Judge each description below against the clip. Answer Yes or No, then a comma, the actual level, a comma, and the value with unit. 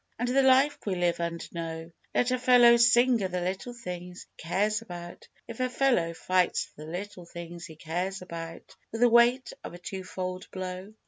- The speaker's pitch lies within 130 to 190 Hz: Yes, medium, 185 Hz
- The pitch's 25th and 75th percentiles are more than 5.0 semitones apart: Yes, wide, 5.5 semitones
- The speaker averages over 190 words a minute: Yes, average, 200 wpm